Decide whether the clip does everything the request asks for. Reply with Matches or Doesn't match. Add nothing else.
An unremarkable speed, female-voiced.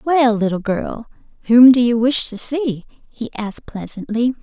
Matches